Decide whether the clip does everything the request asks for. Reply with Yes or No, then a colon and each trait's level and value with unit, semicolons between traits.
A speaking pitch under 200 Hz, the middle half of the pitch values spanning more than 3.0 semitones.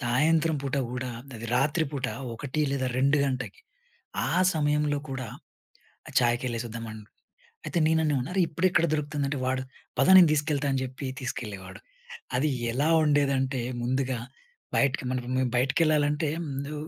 No: medium, 140 Hz; average, 2.7 semitones